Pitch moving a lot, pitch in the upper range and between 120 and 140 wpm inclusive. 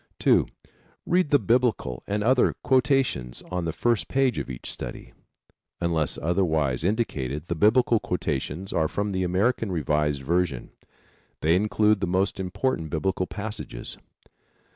No: wide, 5.9 semitones; very low, 90 Hz; slow, 135 wpm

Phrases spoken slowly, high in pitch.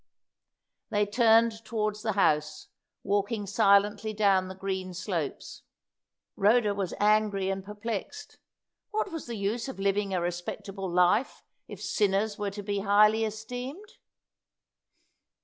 Yes: slow, 125 wpm; high, 205 Hz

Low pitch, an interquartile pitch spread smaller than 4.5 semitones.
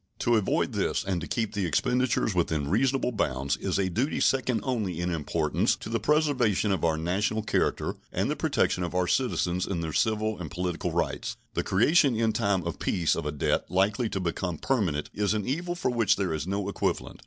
No: low, 100 Hz; average, 4.9 semitones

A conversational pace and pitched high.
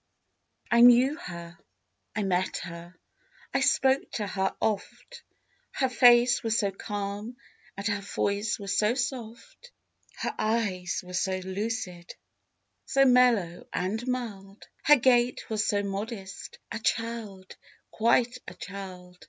No: slow, 130 wpm; high, 215 Hz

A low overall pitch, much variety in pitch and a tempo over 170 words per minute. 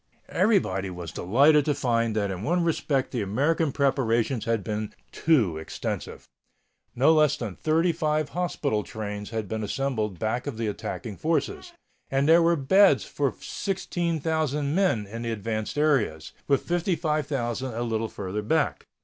No: low, 130 Hz; wide, 6.2 semitones; average, 150 wpm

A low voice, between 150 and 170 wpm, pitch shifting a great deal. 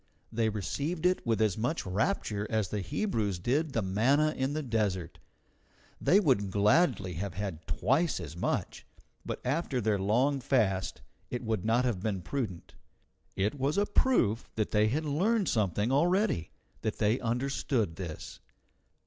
Yes: low, 110 Hz; average, 155 wpm; wide, 5.9 semitones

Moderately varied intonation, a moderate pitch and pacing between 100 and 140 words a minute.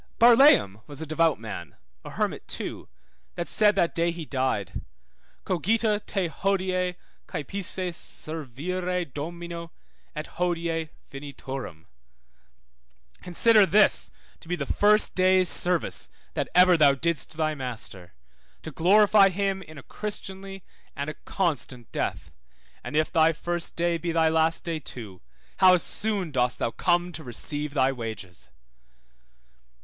Yes: average, 4.5 semitones; medium, 165 Hz; slow, 135 wpm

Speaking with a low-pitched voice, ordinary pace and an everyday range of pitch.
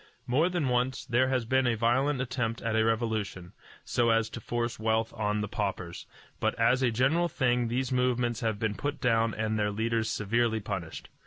No: low, 115 Hz; average, 190 wpm; narrow, 2.3 semitones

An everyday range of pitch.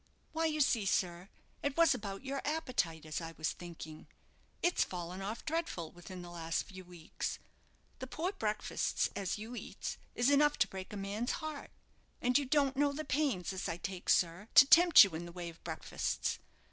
No: wide, 8.4 semitones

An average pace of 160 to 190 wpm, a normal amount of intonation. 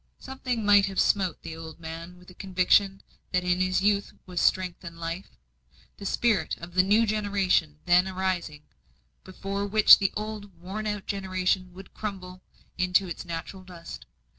No: average, 165 wpm; narrow, 2.0 semitones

